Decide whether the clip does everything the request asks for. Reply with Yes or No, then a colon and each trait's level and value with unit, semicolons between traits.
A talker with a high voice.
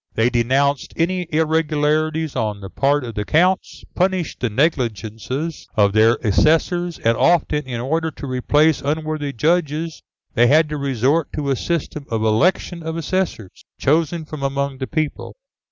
No: medium, 150 Hz